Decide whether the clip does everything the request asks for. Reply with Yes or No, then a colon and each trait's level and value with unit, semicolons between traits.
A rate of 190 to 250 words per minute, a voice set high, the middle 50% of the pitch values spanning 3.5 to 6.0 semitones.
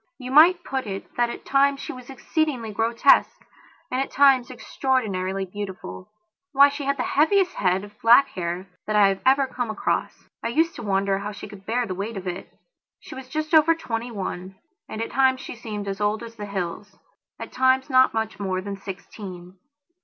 Yes: average, 200 wpm; high, 225 Hz; average, 5.2 semitones